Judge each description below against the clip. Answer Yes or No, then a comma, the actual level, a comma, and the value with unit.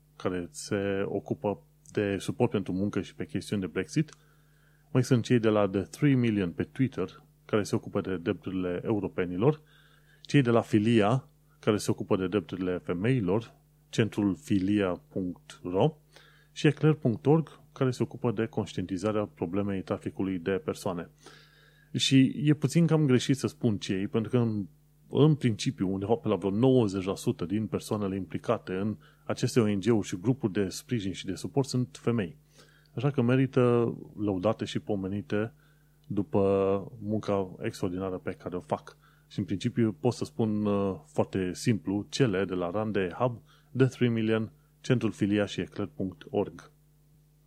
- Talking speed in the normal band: Yes, average, 145 wpm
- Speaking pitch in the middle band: No, low, 115 Hz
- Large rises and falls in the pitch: Yes, wide, 6.0 semitones